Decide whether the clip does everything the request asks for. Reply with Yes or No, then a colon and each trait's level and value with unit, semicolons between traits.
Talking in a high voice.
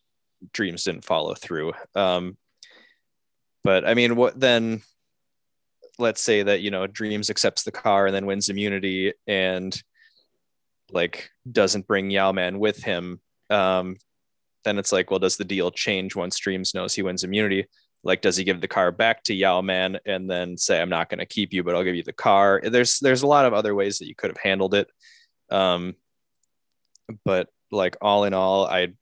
No: low, 100 Hz